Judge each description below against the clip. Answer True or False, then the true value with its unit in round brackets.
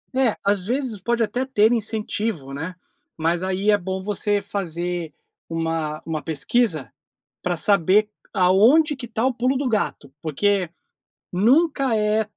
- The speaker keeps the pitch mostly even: False (5.1 semitones)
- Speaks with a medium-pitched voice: False (205 Hz)